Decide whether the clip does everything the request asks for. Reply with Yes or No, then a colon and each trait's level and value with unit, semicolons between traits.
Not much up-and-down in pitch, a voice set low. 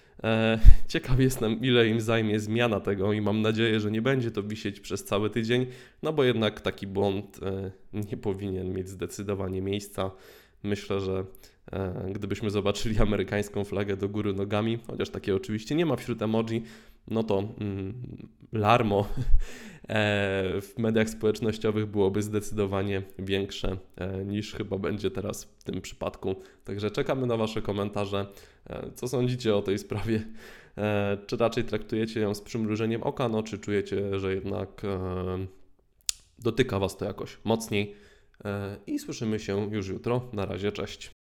Yes: narrow, 2.3 semitones; low, 105 Hz